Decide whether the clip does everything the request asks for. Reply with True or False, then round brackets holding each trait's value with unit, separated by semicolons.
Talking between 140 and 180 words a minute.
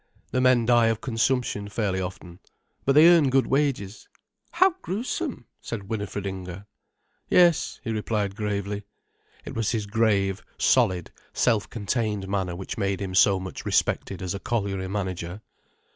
True (145 wpm)